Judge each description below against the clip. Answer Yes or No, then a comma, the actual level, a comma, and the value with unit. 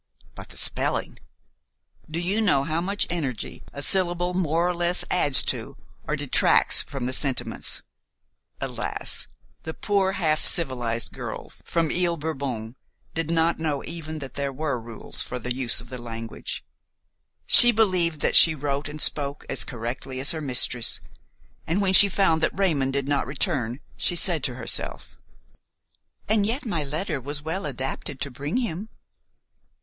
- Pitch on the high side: No, medium, 155 Hz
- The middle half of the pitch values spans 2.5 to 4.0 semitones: No, average, 4.7 semitones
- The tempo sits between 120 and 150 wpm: No, average, 160 wpm